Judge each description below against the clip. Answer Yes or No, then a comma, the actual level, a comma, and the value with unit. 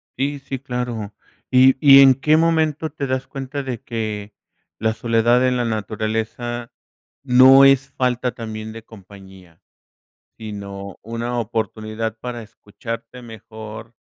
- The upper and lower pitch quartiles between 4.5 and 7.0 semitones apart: No, average, 3.2 semitones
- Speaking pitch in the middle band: No, low, 115 Hz